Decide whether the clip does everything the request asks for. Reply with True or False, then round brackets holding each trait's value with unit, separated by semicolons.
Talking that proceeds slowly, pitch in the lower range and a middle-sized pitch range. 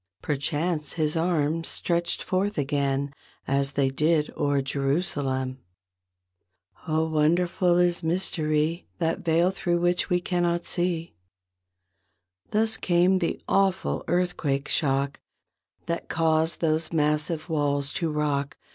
False (110 wpm; 160 Hz; 3.3 semitones)